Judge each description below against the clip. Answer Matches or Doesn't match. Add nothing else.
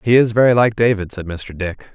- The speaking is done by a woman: Doesn't match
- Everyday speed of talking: Doesn't match